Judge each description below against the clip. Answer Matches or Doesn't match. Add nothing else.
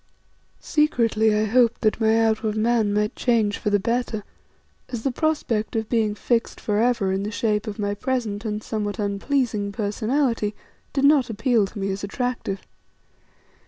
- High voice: Matches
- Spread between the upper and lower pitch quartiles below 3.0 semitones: Matches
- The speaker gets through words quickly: Doesn't match